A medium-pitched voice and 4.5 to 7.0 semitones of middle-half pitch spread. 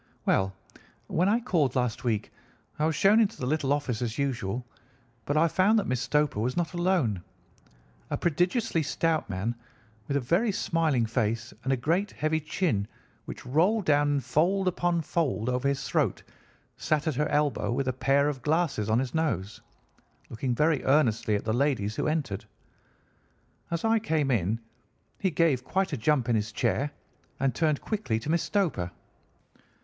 Yes: medium, 145 Hz; wide, 5.6 semitones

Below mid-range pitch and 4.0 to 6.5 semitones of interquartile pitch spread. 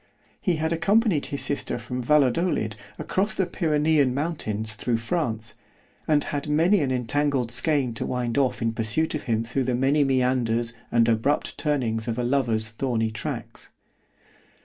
Yes: low, 130 Hz; average, 4.6 semitones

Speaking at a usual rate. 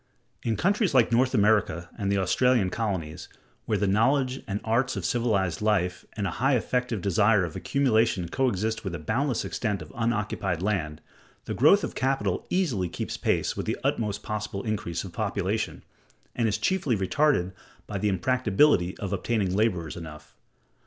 Yes: average, 165 wpm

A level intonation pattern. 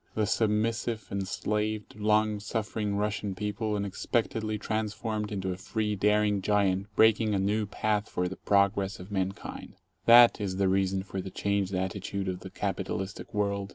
Yes: narrow, 1.7 semitones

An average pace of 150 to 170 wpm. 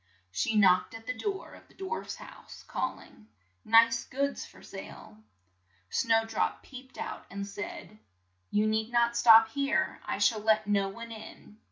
Yes: average, 165 wpm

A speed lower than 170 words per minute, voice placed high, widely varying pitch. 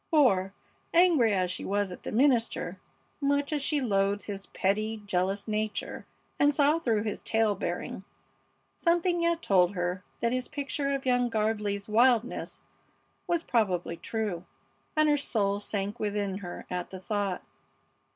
Yes: average, 150 wpm; high, 215 Hz; wide, 5.8 semitones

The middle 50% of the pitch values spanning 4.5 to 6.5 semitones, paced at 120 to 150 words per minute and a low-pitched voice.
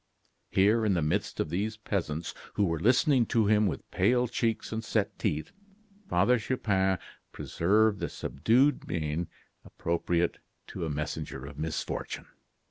Yes: average, 5.1 semitones; average, 145 wpm; low, 100 Hz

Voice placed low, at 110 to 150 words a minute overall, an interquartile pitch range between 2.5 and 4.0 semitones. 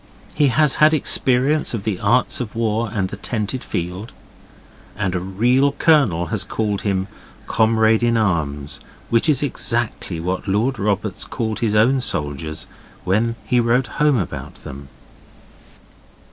No: low, 110 Hz; average, 145 wpm; average, 4.6 semitones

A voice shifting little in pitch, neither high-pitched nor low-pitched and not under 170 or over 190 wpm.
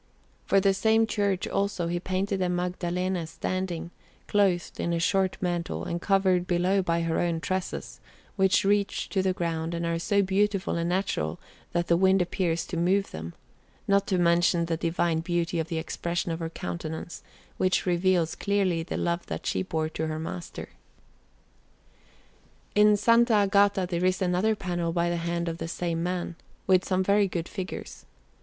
Yes: narrow, 2.3 semitones; medium, 180 Hz; average, 175 wpm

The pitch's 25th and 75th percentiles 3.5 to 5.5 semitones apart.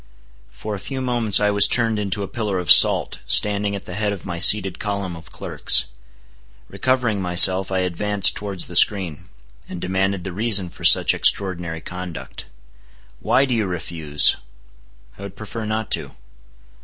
No: average, 2.7 semitones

